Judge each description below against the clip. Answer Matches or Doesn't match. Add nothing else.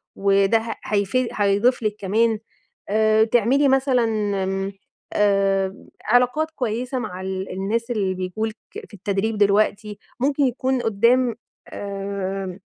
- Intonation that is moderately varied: Matches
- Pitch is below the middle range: Doesn't match